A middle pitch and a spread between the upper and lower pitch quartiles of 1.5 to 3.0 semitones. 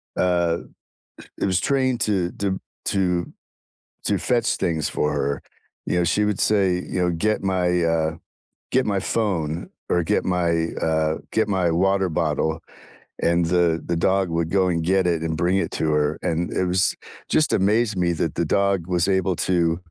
No: very low, 90 Hz; narrow, 2.6 semitones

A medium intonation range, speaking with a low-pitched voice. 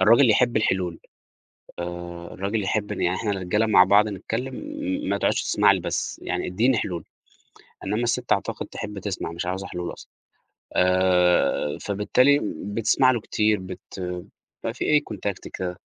Yes: average, 3.3 semitones; very low, 95 Hz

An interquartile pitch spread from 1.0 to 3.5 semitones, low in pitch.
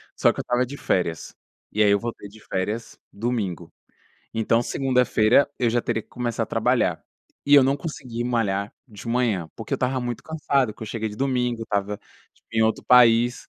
Yes: average, 2.7 semitones; low, 115 Hz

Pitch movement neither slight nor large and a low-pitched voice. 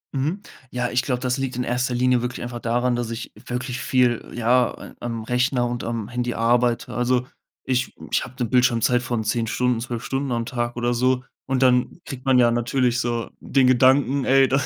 No: narrow, 1.1 semitones; low, 125 Hz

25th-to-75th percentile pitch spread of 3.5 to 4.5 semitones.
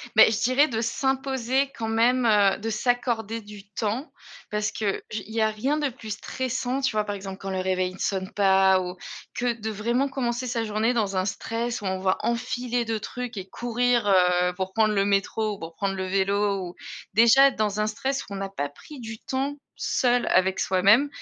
Yes: average, 3.8 semitones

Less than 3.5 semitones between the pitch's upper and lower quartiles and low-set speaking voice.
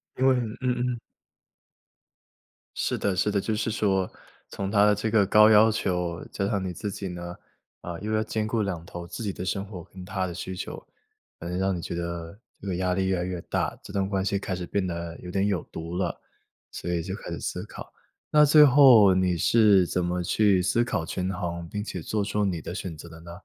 Yes: average, 3.0 semitones; very low, 95 Hz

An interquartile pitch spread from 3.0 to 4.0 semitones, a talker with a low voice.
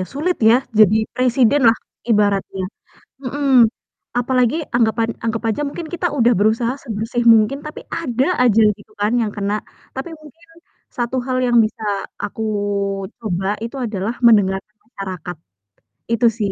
No: average, 3.3 semitones; high, 230 Hz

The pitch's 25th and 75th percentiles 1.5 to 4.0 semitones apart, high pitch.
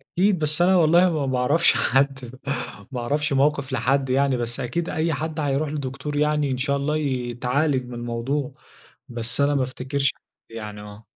No: average, 3.1 semitones; medium, 140 Hz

